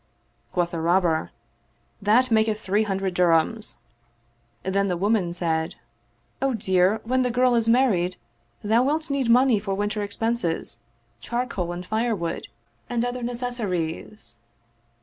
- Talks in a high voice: Yes, high, 210 Hz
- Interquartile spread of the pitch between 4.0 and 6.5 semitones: Yes, average, 5.0 semitones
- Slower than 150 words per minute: Yes, average, 140 wpm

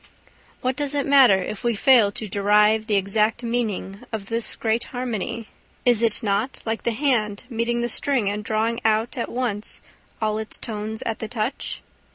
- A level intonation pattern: Yes, narrow, 2.3 semitones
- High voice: Yes, high, 220 Hz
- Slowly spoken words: No, average, 180 wpm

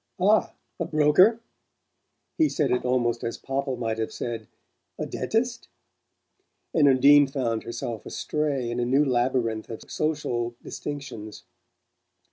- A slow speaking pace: Yes, slow, 125 wpm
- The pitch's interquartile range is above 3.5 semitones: Yes, average, 4.0 semitones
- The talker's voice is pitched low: Yes, low, 130 Hz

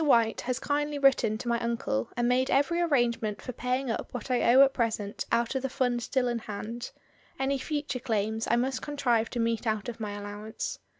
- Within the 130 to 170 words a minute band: No, fast, 205 wpm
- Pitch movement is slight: No, average, 3.0 semitones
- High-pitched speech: Yes, high, 240 Hz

